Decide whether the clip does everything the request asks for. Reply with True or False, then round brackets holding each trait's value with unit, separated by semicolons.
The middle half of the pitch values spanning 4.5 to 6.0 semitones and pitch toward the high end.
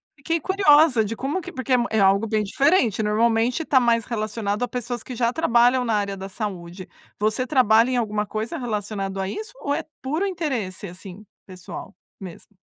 False (4.1 semitones; 230 Hz)